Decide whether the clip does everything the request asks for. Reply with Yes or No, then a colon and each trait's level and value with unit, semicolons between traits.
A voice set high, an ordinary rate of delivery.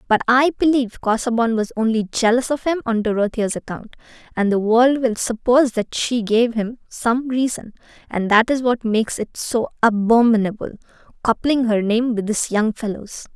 Yes: high, 230 Hz; average, 165 wpm